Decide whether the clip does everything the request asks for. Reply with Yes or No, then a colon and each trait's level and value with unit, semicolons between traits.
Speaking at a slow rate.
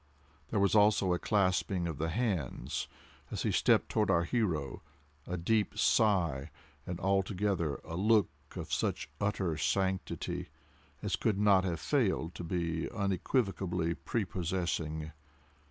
Yes: slow, 120 wpm